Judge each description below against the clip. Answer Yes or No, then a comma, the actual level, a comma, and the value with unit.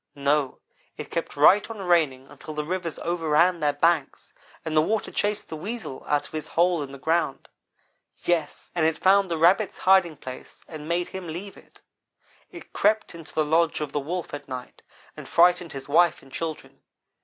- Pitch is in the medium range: Yes, medium, 165 Hz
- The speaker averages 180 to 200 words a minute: Yes, average, 190 wpm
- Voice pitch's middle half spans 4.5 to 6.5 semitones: No, average, 3.1 semitones